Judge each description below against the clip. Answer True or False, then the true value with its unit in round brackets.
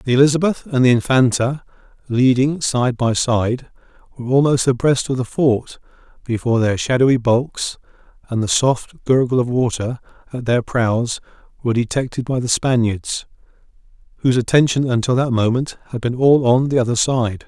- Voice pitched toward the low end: True (125 Hz)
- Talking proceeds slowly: False (155 wpm)